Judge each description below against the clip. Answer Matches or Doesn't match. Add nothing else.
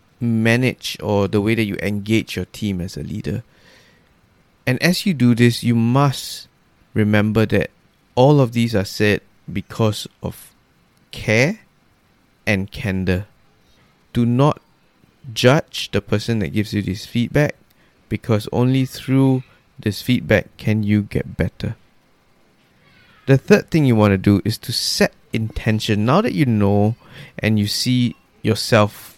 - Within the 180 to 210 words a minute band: Doesn't match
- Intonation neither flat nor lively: Matches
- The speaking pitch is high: Doesn't match